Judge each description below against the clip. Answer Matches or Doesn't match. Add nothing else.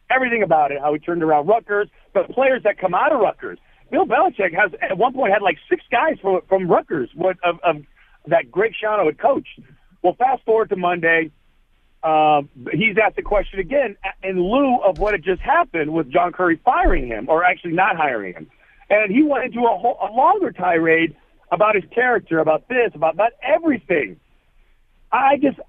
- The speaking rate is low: Doesn't match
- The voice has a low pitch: Doesn't match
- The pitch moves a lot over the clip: Matches